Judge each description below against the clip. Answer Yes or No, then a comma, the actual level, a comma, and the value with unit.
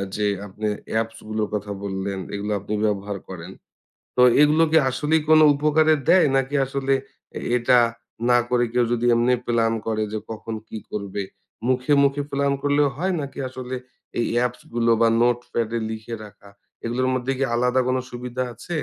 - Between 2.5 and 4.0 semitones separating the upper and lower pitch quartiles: Yes, average, 3.7 semitones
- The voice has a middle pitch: No, low, 120 Hz